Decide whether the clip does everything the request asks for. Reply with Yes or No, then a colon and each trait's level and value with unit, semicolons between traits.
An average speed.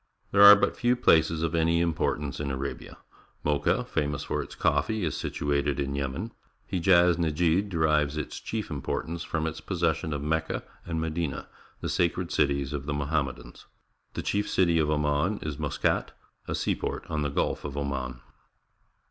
Yes: average, 175 wpm